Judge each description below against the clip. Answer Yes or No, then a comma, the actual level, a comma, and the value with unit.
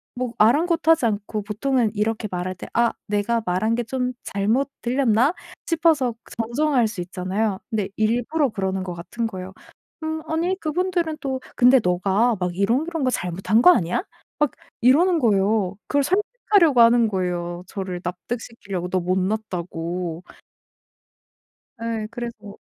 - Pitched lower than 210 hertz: No, high, 225 Hz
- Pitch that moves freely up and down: Yes, wide, 5.8 semitones